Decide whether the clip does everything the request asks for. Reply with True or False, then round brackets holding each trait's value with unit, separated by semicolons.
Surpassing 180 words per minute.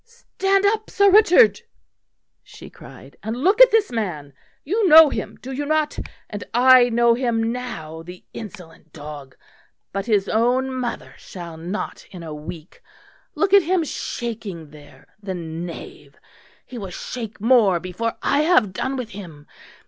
False (155 wpm)